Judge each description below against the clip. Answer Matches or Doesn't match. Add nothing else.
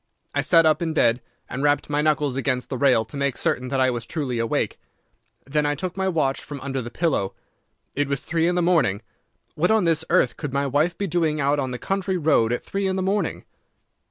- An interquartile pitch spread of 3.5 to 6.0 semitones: Matches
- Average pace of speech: Doesn't match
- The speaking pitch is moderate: Matches